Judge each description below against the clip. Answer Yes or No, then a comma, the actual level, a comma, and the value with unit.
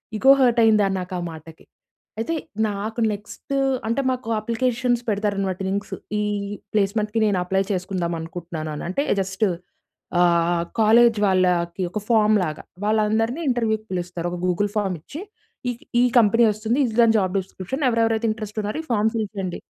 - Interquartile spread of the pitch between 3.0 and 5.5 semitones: Yes, average, 3.5 semitones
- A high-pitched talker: Yes, high, 210 Hz